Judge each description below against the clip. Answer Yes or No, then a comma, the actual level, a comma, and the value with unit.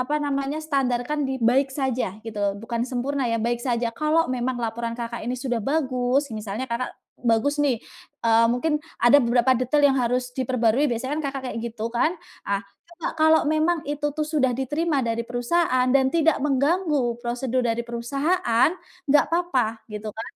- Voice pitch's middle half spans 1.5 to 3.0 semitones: No, average, 3.6 semitones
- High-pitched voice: Yes, very high, 255 Hz